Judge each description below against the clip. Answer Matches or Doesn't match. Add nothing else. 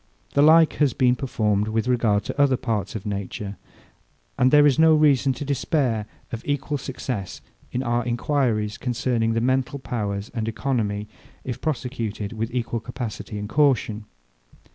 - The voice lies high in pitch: Doesn't match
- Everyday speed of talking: Matches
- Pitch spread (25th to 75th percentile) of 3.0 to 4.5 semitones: Matches